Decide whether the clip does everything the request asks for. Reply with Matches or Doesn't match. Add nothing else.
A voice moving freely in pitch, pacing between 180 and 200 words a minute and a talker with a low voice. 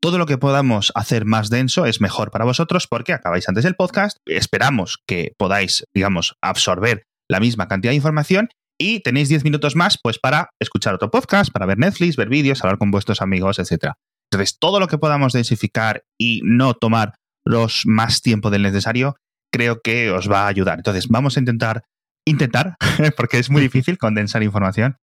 Matches